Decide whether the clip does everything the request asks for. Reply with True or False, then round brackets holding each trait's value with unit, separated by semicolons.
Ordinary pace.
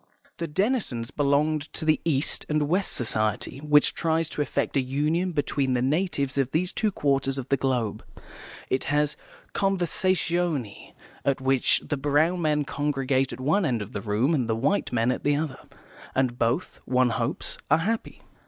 True (170 wpm)